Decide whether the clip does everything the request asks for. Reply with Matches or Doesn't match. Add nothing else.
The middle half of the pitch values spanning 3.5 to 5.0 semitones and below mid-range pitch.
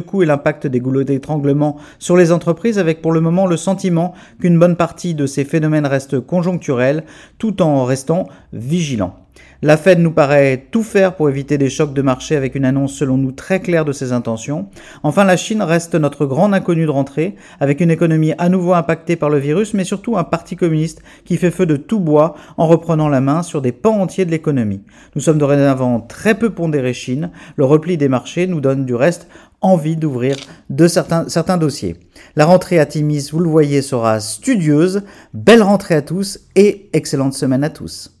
Doesn't match